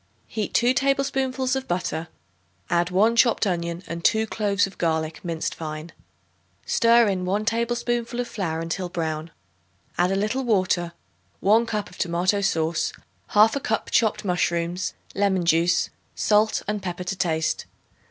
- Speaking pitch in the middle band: No, high, 195 Hz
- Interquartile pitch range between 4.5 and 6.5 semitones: Yes, average, 4.8 semitones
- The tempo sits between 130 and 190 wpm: Yes, average, 145 wpm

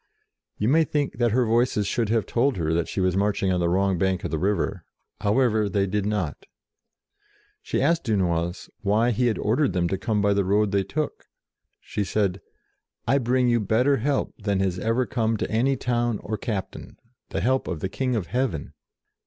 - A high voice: No, low, 105 Hz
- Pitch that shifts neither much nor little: Yes, average, 4.2 semitones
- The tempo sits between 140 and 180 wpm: No, average, 195 wpm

